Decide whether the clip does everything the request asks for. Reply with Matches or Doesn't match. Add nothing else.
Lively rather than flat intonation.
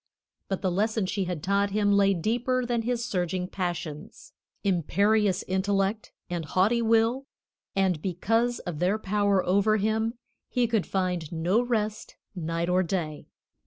Doesn't match